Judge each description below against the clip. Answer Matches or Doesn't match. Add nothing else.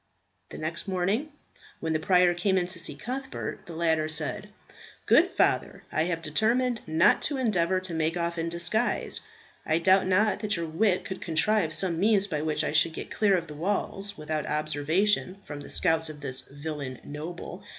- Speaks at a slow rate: Doesn't match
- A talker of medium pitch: Matches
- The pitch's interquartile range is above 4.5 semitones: Doesn't match